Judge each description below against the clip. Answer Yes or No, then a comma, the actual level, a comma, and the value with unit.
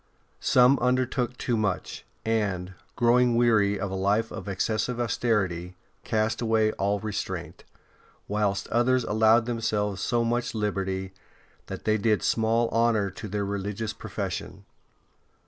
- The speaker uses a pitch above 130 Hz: No, low, 110 Hz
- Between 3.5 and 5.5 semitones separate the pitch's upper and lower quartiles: No, average, 2.8 semitones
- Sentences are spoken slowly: Yes, slow, 130 wpm